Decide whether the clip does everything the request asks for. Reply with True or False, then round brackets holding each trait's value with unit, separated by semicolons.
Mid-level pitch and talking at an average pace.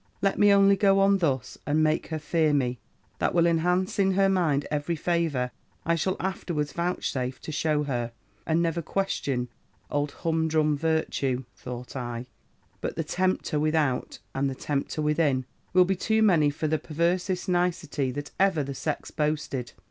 True (155 Hz; 165 wpm)